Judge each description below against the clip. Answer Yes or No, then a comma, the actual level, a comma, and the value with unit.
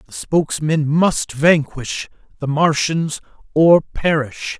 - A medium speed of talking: No, slow, 105 wpm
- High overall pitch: No, medium, 155 Hz